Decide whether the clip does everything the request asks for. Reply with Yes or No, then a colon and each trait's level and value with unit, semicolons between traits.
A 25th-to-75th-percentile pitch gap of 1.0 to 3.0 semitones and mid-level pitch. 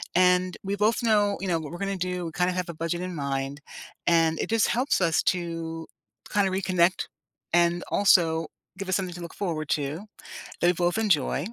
Yes: average, 2.7 semitones; medium, 175 Hz